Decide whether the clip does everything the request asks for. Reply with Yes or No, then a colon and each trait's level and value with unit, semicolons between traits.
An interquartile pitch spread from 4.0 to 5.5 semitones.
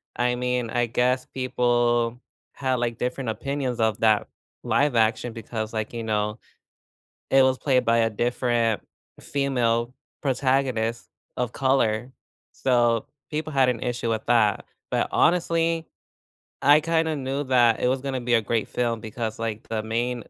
No: narrow, 2.4 semitones